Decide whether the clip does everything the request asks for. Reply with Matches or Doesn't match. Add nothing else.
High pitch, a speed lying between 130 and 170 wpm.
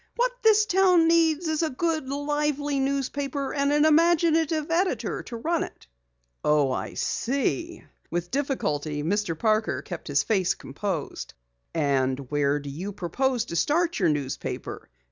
Matches